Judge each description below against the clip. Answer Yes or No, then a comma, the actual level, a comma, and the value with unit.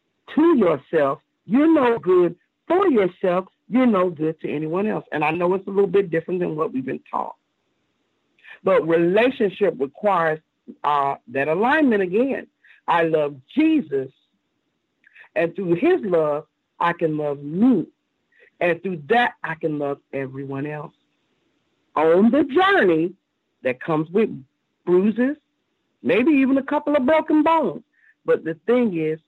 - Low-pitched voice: No, high, 190 Hz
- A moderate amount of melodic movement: No, wide, 9.0 semitones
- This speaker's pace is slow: No, average, 145 wpm